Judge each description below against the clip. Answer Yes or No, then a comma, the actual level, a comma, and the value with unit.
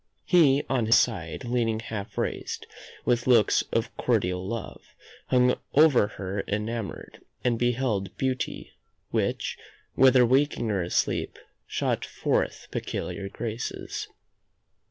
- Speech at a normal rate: No, slow, 115 wpm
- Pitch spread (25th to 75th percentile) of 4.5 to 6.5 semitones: No, average, 3.6 semitones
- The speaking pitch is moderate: No, low, 115 Hz